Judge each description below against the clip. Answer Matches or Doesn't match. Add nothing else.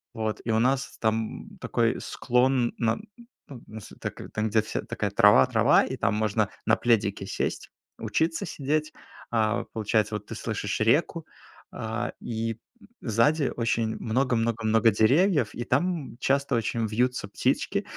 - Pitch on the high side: Doesn't match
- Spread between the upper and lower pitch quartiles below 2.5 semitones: Doesn't match